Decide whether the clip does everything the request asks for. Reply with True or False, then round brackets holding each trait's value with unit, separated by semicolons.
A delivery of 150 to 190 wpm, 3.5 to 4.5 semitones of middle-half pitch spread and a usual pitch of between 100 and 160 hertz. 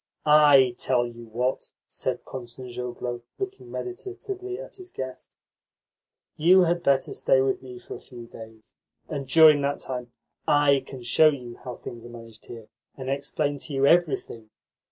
True (155 wpm; 3.9 semitones; 135 Hz)